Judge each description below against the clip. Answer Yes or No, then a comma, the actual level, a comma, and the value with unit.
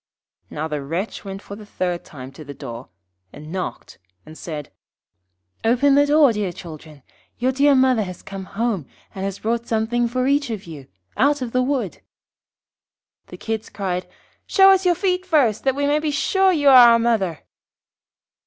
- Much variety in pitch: Yes, wide, 7.6 semitones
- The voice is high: Yes, high, 225 Hz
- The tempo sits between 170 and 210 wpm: Yes, average, 175 wpm